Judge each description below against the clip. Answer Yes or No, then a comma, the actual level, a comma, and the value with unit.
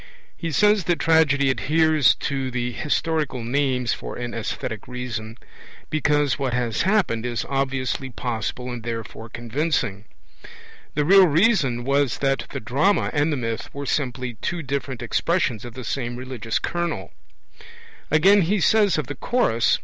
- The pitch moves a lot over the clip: No, average, 4.7 semitones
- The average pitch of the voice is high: No, low, 135 Hz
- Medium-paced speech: Yes, average, 155 wpm